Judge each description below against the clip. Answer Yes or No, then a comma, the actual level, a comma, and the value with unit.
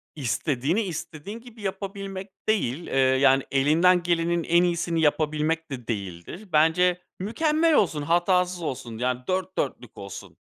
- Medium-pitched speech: Yes, medium, 165 Hz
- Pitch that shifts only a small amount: No, wide, 5.6 semitones